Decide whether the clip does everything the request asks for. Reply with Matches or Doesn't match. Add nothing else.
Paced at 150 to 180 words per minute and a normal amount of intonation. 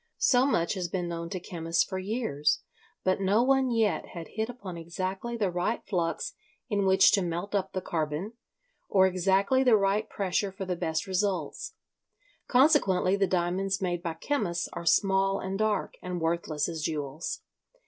Matches